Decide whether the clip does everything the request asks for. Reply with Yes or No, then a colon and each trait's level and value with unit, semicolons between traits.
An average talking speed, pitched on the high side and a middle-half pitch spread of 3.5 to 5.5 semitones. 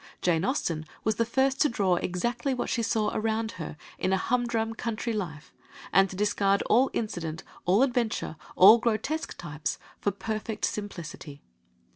Yes: average, 155 wpm; high, 215 Hz; average, 4.4 semitones